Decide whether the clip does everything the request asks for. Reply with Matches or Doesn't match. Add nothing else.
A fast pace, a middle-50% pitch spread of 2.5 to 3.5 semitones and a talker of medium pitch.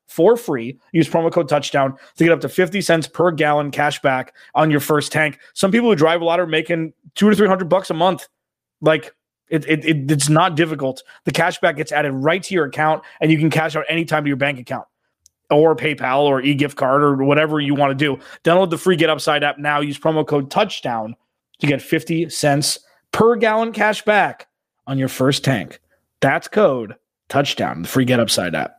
Matches